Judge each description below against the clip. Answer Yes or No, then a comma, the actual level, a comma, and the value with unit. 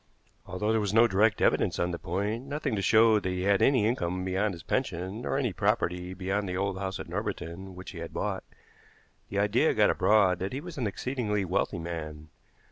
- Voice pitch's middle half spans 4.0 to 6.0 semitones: No, average, 3.3 semitones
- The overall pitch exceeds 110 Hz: No, low, 100 Hz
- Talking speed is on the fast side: Yes, fast, 210 wpm